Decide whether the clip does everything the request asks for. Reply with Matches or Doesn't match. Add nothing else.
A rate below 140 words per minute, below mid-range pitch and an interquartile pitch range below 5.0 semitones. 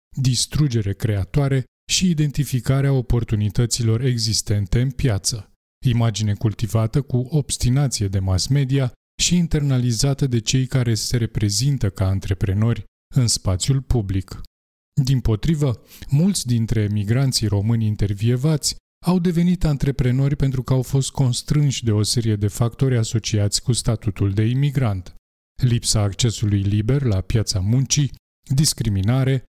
Matches